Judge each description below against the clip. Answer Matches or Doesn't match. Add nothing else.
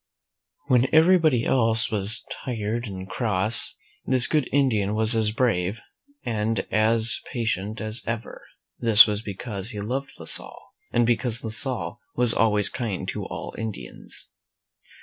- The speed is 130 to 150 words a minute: Matches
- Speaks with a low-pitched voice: Matches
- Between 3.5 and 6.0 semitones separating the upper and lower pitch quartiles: Doesn't match